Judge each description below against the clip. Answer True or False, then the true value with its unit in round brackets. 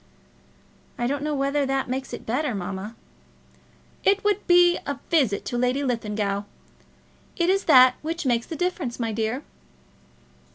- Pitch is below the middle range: False (265 Hz)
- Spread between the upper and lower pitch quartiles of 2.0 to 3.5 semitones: False (5.2 semitones)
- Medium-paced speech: True (155 wpm)